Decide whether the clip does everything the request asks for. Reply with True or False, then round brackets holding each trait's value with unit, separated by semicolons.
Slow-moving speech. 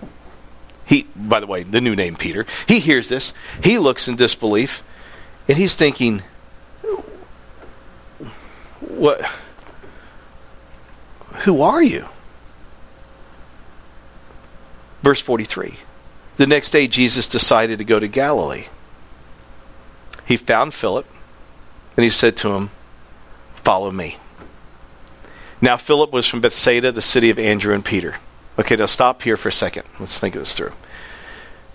True (125 wpm)